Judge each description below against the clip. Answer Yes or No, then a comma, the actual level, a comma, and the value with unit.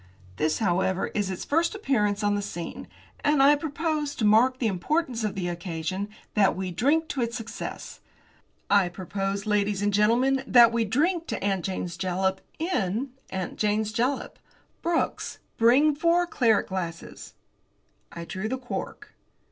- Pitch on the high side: Yes, high, 215 Hz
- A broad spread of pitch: Yes, wide, 6.0 semitones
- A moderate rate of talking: Yes, average, 155 wpm